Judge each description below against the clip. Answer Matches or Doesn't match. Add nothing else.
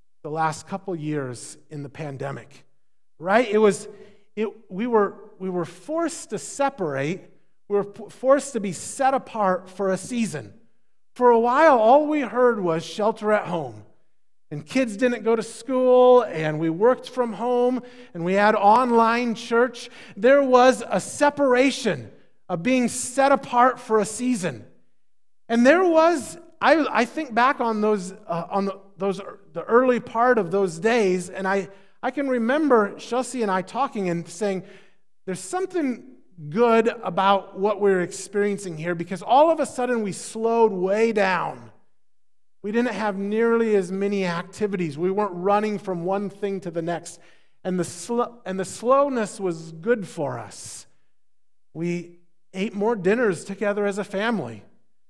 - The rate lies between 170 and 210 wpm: Doesn't match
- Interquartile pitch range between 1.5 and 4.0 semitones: Doesn't match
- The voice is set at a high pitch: Matches